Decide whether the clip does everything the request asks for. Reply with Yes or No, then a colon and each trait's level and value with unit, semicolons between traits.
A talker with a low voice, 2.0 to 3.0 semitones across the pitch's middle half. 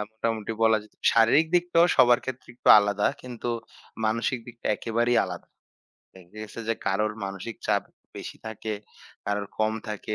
Yes: low, 110 Hz; narrow, 2.6 semitones